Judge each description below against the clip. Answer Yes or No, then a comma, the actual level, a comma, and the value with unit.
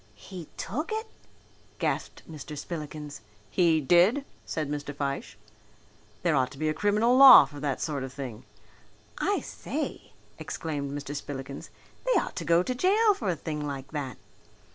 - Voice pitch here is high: No, medium, 150 Hz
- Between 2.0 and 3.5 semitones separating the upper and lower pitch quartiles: No, average, 5.1 semitones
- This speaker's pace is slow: No, average, 160 wpm